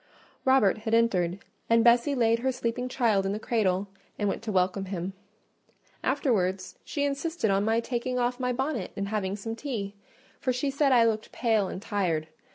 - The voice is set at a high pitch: Yes, high, 225 Hz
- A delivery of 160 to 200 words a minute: Yes, average, 180 wpm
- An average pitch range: Yes, average, 4.1 semitones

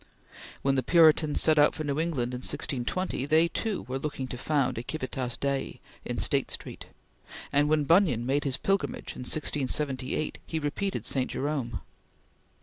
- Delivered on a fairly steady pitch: No, average, 3.3 semitones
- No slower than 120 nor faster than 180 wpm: Yes, average, 160 wpm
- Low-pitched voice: No, medium, 145 Hz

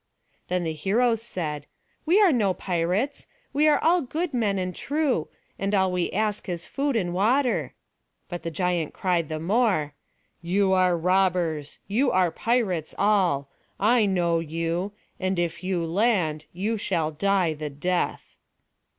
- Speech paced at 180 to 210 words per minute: No, average, 150 wpm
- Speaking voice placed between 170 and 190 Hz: Yes, medium, 185 Hz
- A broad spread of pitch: No, average, 4.6 semitones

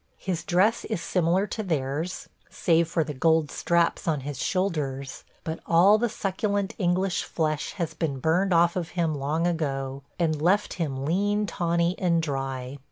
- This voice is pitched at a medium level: Yes, medium, 170 Hz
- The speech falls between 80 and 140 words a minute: No, average, 165 wpm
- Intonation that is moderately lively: Yes, average, 3.6 semitones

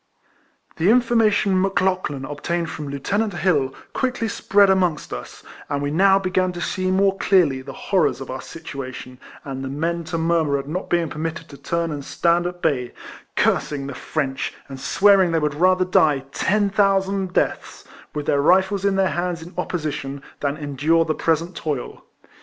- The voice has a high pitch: No, medium, 170 Hz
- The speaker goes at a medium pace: Yes, average, 175 wpm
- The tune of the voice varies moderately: Yes, average, 4.7 semitones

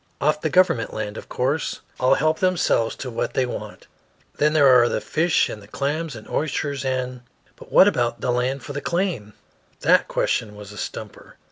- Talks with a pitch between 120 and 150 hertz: Yes, low, 135 Hz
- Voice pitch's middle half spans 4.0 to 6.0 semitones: Yes, average, 4.5 semitones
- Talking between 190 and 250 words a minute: Yes, average, 200 wpm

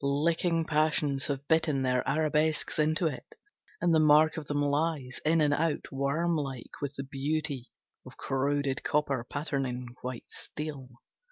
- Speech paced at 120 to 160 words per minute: Yes, average, 150 wpm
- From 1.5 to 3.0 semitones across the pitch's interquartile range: Yes, narrow, 2.5 semitones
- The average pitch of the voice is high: No, medium, 145 Hz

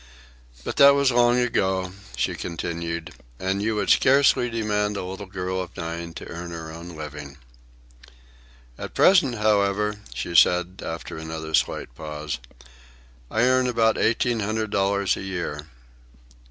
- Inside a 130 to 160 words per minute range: Yes, average, 140 wpm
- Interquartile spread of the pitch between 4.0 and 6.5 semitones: Yes, average, 4.9 semitones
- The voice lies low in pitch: Yes, very low, 95 Hz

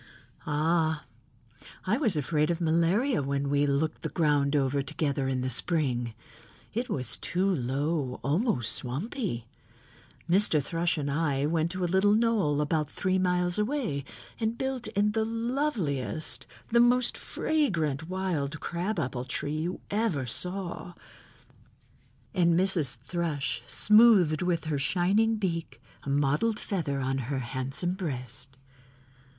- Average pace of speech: No, slow, 130 wpm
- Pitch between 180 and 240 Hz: No, medium, 165 Hz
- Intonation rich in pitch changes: Yes, wide, 5.7 semitones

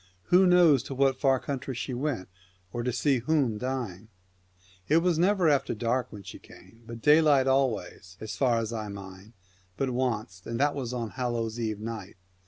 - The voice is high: No, low, 125 Hz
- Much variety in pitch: No, average, 4.0 semitones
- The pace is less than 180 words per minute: No, average, 190 wpm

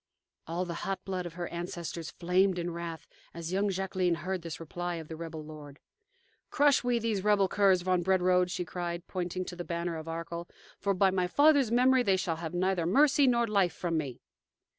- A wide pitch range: No, narrow, 2.4 semitones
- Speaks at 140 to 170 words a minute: No, average, 200 wpm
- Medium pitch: Yes, medium, 180 Hz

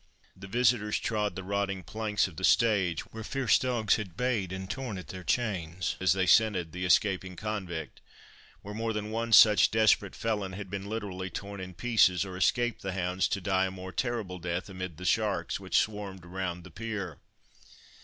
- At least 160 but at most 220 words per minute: Yes, average, 185 wpm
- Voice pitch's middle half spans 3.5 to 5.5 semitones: No, average, 2.9 semitones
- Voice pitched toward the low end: Yes, low, 100 Hz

